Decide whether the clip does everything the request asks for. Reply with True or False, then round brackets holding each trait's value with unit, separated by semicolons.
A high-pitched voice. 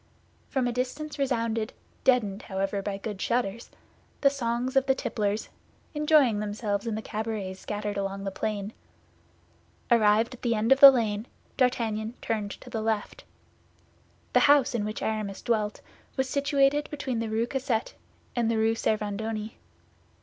True (225 Hz)